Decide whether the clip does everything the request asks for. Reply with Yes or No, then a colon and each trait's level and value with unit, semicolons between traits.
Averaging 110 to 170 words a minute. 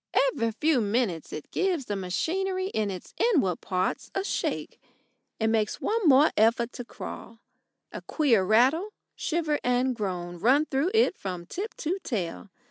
Yes: average, 155 wpm